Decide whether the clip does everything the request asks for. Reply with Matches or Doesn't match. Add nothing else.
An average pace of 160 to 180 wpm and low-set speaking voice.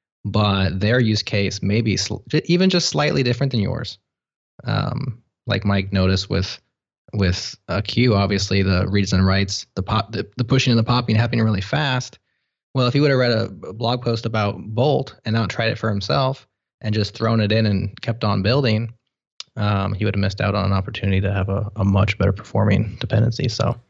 Doesn't match